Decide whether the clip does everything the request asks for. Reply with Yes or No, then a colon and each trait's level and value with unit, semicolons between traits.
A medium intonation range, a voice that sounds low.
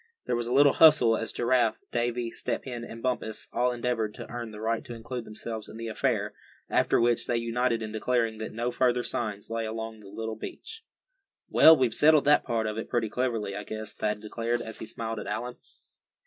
No: narrow, 1.9 semitones; low, 115 Hz